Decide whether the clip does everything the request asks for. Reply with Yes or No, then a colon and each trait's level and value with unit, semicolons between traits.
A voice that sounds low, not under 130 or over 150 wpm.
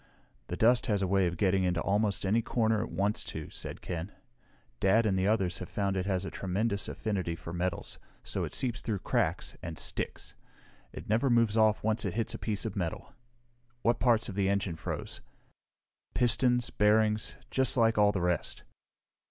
No: low, 105 Hz; average, 185 wpm